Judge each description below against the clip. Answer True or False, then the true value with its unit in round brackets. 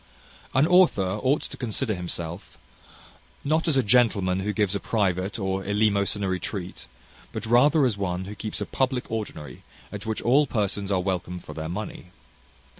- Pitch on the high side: False (105 Hz)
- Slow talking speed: False (165 wpm)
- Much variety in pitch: False (4.5 semitones)